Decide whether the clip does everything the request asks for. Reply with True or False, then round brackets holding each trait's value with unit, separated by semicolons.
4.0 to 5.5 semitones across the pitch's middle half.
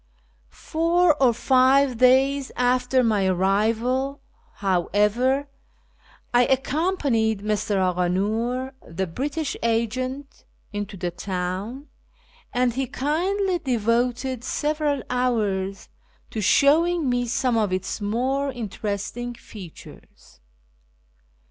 True (4.7 semitones)